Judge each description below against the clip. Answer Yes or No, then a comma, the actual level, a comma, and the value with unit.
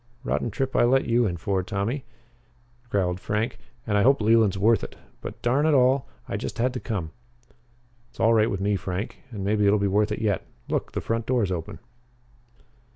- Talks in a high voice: No, low, 110 Hz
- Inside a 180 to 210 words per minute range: Yes, average, 200 wpm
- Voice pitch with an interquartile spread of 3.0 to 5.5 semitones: Yes, average, 3.3 semitones